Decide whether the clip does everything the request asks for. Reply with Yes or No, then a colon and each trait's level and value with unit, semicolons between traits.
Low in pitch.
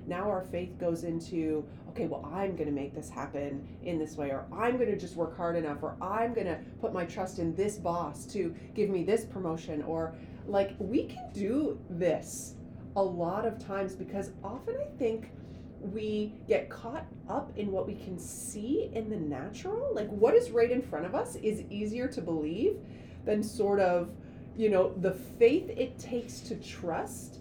No: high, 195 Hz